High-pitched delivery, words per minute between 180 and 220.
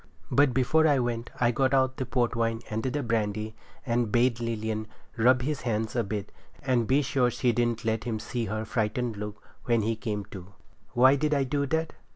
No: low, 120 Hz; average, 200 wpm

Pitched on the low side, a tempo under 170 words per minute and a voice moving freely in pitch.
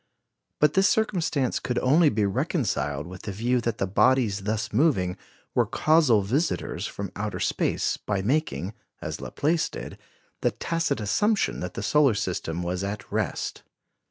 Yes: low, 115 Hz; average, 155 wpm; wide, 7.4 semitones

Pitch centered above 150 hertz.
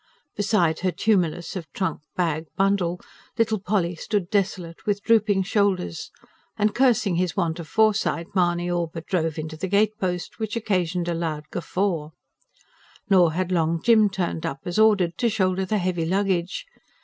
Yes: medium, 185 Hz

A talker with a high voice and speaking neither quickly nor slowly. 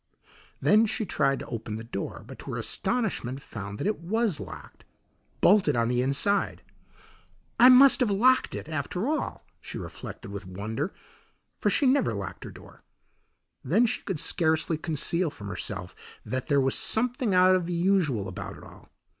No: medium, 165 Hz; average, 170 wpm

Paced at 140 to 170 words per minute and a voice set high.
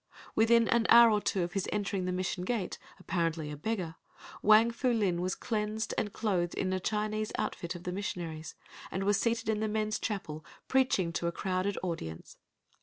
No: average, 185 wpm; high, 195 Hz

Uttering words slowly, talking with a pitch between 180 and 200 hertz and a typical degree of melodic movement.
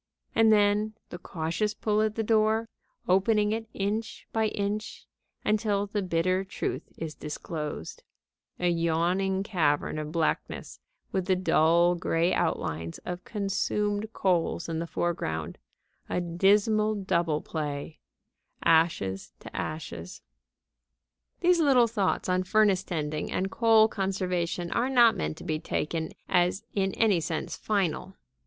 Yes: slow, 130 wpm; medium, 185 Hz; average, 4.3 semitones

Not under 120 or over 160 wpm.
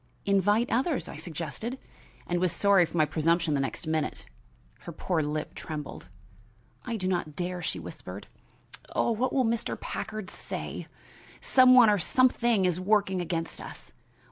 Yes: average, 155 wpm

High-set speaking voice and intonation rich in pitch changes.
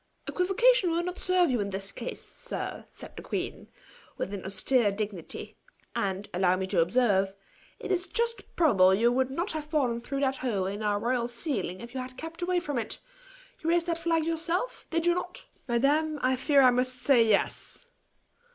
Yes: very high, 255 Hz; wide, 8.2 semitones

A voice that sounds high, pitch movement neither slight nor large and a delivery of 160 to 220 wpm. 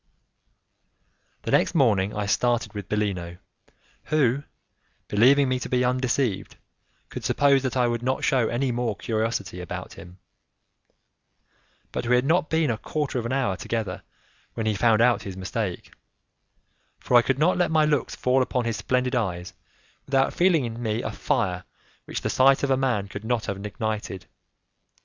No: low, 120 Hz; average, 4.1 semitones; average, 170 wpm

